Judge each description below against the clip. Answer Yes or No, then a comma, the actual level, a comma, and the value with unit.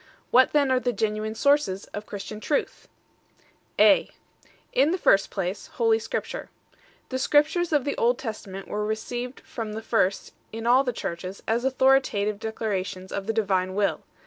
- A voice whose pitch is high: Yes, high, 220 Hz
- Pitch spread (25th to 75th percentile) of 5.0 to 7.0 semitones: No, average, 4.2 semitones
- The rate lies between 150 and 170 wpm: Yes, average, 165 wpm